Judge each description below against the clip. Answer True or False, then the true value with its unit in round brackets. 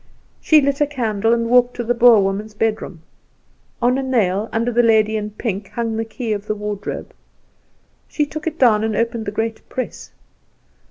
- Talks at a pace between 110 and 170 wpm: False (185 wpm)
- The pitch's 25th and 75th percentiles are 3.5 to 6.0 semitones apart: False (2.5 semitones)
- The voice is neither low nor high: False (225 Hz)